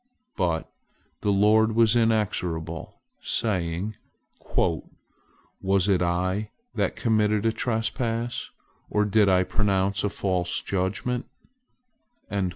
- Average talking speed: No, slow, 95 wpm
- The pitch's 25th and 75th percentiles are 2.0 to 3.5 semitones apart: Yes, average, 3.1 semitones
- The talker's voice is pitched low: Yes, low, 100 Hz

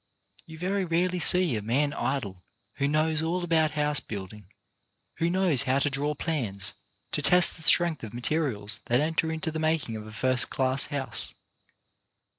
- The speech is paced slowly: No, average, 170 wpm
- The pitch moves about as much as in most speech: Yes, average, 4.9 semitones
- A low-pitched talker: No, medium, 150 Hz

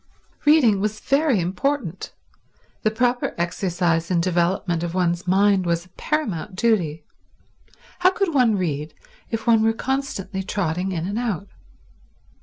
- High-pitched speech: Yes, high, 195 Hz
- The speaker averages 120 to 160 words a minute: Yes, slow, 135 wpm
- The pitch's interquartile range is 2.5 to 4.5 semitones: No, average, 5.2 semitones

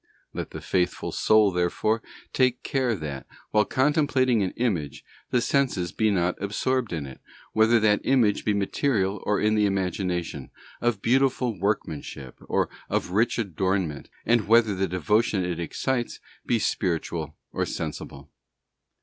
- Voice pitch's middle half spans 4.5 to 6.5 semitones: Yes, average, 4.8 semitones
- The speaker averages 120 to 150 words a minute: Yes, average, 140 wpm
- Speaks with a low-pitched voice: Yes, low, 105 Hz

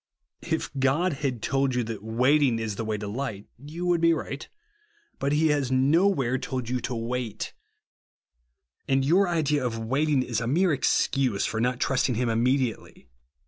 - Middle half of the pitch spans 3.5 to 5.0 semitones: Yes, average, 4.1 semitones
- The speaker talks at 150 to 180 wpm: Yes, average, 175 wpm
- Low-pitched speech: Yes, low, 130 Hz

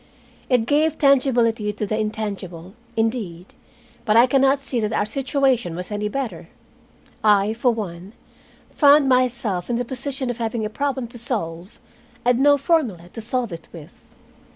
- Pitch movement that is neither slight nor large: Yes, average, 4.1 semitones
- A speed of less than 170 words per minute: Yes, average, 160 wpm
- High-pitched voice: Yes, high, 230 Hz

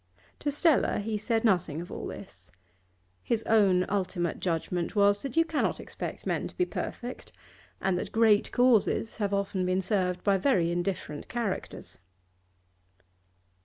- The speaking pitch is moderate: No, high, 200 Hz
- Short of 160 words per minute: Yes, average, 145 wpm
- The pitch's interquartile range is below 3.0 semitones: No, average, 3.9 semitones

